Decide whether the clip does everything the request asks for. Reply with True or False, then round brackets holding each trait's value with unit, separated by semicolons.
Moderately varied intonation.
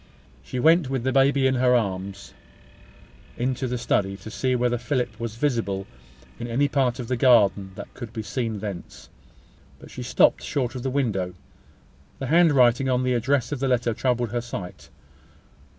True (3.0 semitones)